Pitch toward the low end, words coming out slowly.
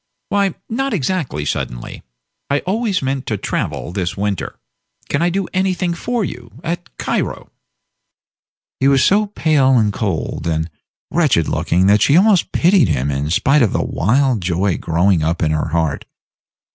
No: low, 130 Hz; average, 160 wpm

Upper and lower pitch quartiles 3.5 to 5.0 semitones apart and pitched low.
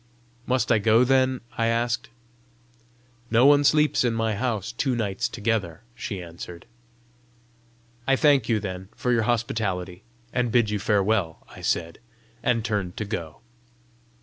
Yes: average, 3.9 semitones; low, 110 Hz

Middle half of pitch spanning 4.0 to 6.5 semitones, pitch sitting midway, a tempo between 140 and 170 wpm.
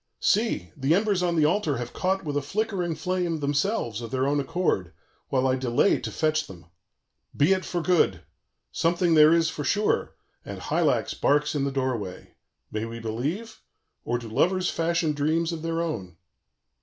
No: average, 5.2 semitones; medium, 155 Hz; average, 180 wpm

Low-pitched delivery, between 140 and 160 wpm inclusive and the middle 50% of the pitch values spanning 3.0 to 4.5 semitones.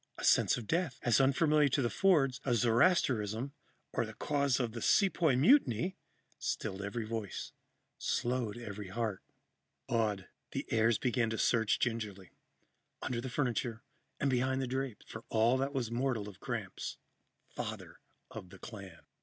Yes: low, 120 Hz; average, 155 wpm; average, 3.4 semitones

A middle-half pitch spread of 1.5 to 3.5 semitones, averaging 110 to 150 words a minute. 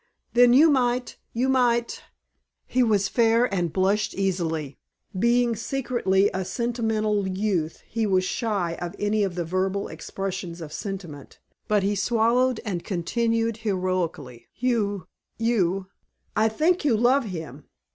No: average, 4.2 semitones; slow, 135 wpm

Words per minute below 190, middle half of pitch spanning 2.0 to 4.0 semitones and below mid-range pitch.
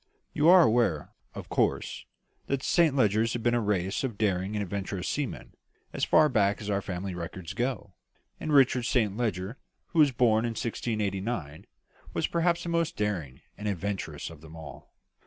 No: average, 175 wpm; average, 4.9 semitones; low, 105 Hz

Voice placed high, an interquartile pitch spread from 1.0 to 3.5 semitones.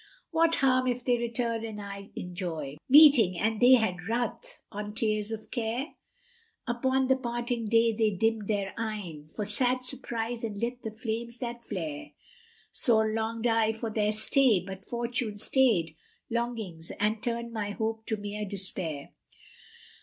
Yes: high, 225 Hz; narrow, 2.6 semitones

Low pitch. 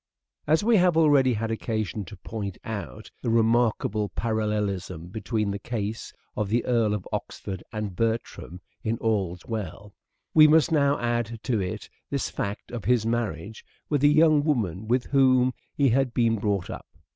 Yes: low, 115 Hz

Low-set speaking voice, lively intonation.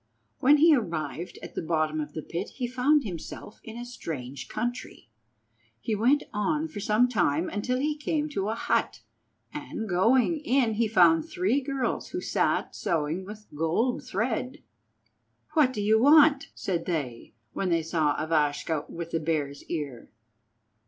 No: high, 205 Hz; wide, 7.9 semitones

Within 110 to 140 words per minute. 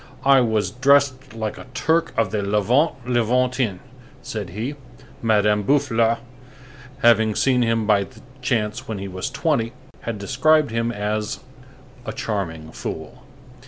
Yes: slow, 135 wpm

